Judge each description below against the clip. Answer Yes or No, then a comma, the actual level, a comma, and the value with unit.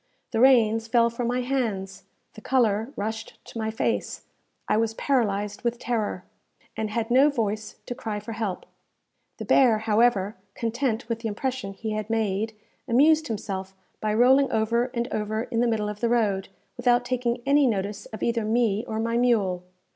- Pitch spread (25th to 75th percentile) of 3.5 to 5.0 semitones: No, narrow, 2.4 semitones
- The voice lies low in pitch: No, high, 225 Hz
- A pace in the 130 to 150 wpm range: No, average, 175 wpm